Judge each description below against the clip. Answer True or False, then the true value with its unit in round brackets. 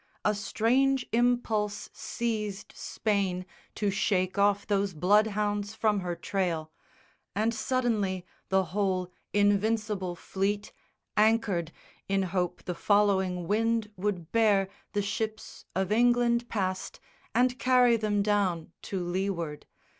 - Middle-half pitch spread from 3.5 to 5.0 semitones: False (2.8 semitones)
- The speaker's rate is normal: False (115 wpm)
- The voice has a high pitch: True (205 Hz)